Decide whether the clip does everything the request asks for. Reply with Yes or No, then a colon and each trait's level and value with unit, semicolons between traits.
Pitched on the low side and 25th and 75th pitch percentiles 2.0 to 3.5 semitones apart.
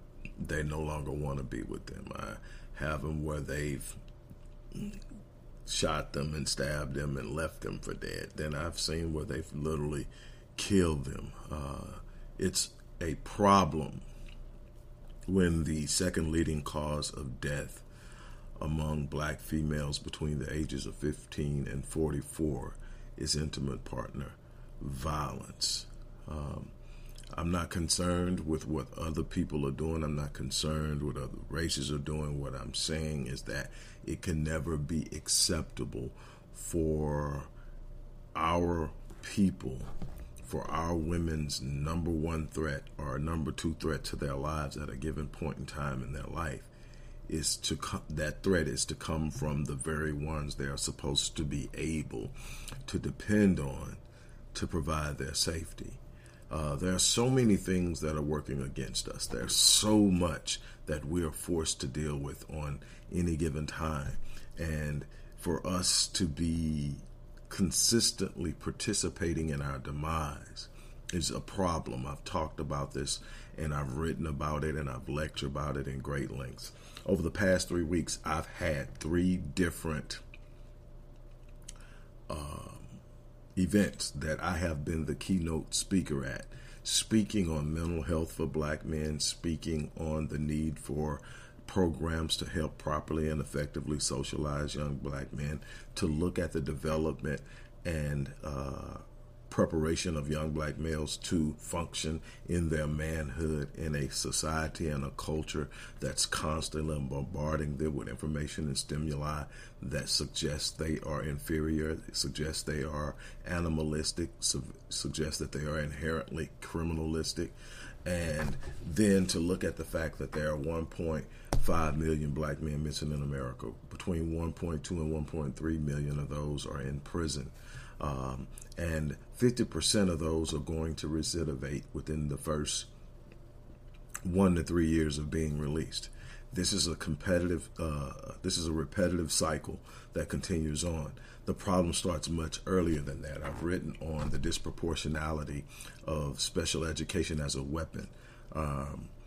Yes: very low, 75 Hz; narrow, 2.5 semitones